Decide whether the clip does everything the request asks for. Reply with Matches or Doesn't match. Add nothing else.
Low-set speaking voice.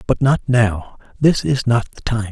Matches